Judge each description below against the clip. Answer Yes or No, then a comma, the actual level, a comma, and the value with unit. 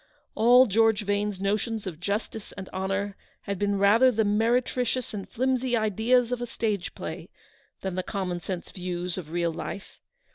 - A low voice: No, high, 205 Hz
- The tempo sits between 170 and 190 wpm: No, average, 160 wpm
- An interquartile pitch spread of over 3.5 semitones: No, average, 3.2 semitones